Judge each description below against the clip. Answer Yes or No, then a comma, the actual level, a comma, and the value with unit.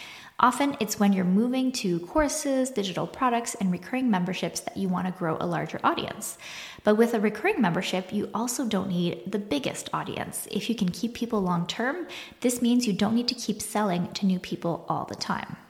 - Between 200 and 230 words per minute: Yes, fast, 205 wpm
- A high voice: Yes, high, 210 Hz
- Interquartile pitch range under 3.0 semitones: No, average, 4.6 semitones